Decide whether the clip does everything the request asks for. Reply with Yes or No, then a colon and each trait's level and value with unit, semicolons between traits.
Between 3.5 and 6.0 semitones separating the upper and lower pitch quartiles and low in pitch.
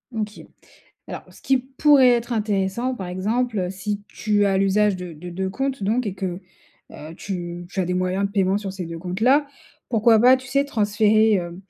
No: average, 4.1 semitones; high, 205 Hz